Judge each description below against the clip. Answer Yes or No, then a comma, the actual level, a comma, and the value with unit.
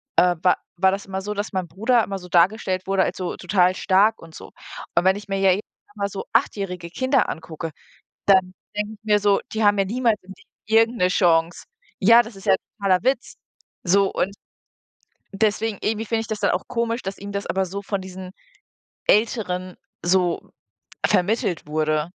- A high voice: Yes, high, 195 Hz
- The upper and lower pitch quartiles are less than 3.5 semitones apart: Yes, average, 2.8 semitones